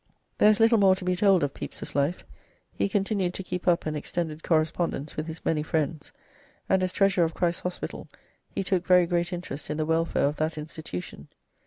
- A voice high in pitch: No, medium, 170 Hz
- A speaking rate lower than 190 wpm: No, average, 200 wpm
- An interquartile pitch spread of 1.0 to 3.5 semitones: Yes, average, 3.0 semitones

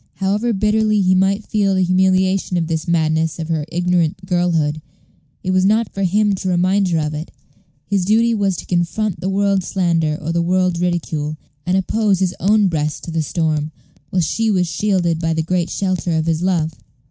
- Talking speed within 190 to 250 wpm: Yes, average, 195 wpm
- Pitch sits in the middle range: Yes, medium, 180 Hz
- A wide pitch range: No, average, 3.0 semitones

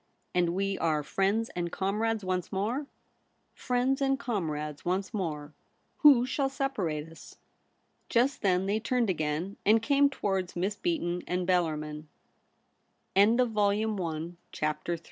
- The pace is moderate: No, slow, 130 wpm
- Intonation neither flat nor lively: No, wide, 5.7 semitones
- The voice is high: Yes, high, 195 Hz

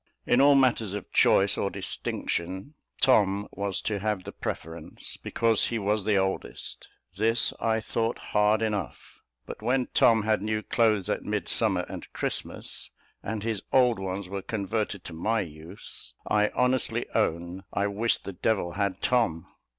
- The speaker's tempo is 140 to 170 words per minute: Yes, average, 155 wpm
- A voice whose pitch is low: Yes, low, 105 Hz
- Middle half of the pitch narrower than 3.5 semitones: Yes, average, 2.7 semitones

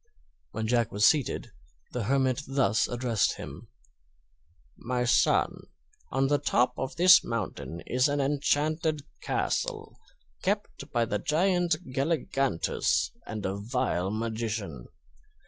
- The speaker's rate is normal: No, slow, 115 wpm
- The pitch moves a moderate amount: Yes, average, 4.6 semitones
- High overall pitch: No, low, 125 Hz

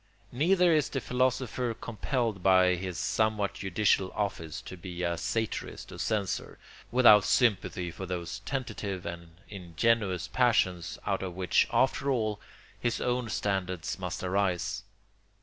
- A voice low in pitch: Yes, low, 100 Hz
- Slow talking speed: Yes, slow, 130 wpm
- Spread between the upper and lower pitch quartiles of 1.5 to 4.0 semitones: No, average, 4.5 semitones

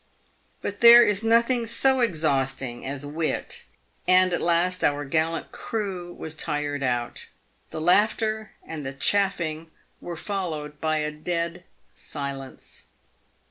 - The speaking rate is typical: No, slow, 125 wpm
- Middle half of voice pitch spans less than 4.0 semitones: No, wide, 5.5 semitones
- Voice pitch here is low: No, medium, 170 Hz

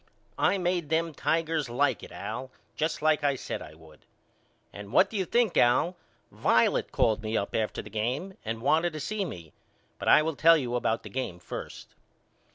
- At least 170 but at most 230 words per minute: Yes, average, 190 wpm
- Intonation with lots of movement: Yes, wide, 6.7 semitones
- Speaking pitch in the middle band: Yes, medium, 145 Hz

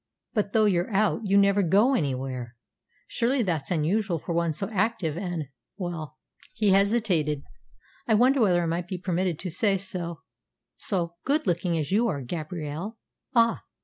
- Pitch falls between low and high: Yes, medium, 180 Hz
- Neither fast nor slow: Yes, average, 160 wpm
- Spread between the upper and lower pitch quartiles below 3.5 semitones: No, average, 4.3 semitones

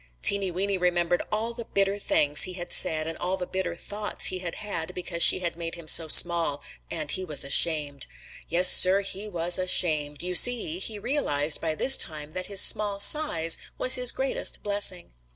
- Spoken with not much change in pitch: No, average, 3.5 semitones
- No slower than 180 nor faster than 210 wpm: Yes, average, 190 wpm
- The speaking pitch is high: No, medium, 180 Hz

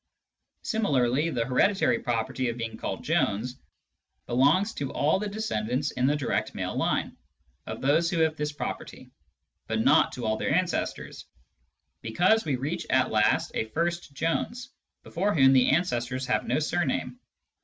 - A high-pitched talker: No, medium, 140 Hz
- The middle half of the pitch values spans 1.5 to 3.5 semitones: No, wide, 5.6 semitones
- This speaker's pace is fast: No, average, 155 wpm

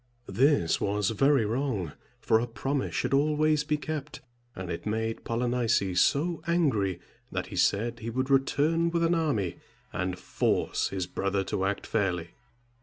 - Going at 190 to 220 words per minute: No, average, 155 wpm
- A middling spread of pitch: No, wide, 7.0 semitones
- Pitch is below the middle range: Yes, low, 120 Hz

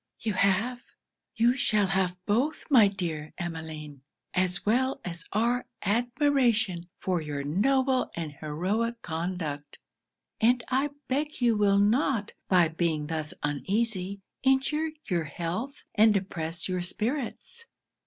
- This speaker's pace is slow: Yes, slow, 125 wpm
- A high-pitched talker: Yes, high, 200 Hz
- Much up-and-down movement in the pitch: Yes, wide, 6.2 semitones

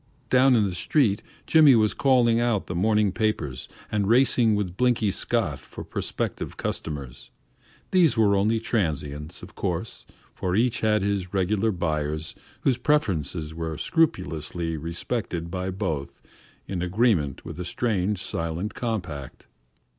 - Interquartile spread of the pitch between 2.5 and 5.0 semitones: No, wide, 5.6 semitones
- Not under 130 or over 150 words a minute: Yes, slow, 135 wpm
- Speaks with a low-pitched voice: Yes, low, 100 Hz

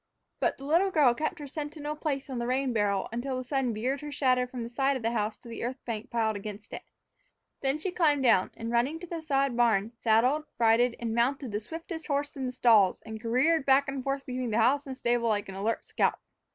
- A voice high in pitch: Yes, very high, 255 Hz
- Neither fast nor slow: No, fast, 230 wpm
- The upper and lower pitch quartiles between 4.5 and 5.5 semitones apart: No, average, 3.6 semitones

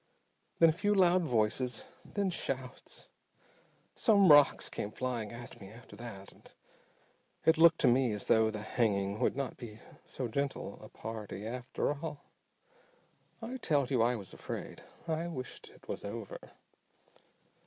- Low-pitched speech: Yes, low, 125 Hz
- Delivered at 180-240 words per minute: No, average, 150 wpm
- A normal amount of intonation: No, wide, 6.1 semitones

